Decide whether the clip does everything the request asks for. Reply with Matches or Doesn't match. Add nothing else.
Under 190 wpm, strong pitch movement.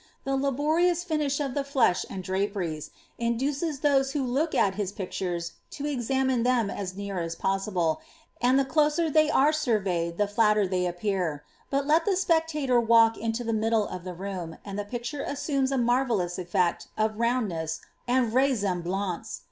Matches